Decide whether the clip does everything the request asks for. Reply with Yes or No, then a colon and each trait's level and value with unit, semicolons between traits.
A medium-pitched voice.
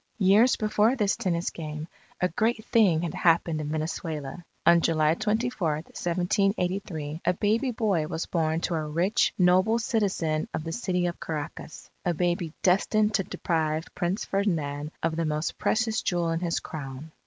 Yes: medium, 175 Hz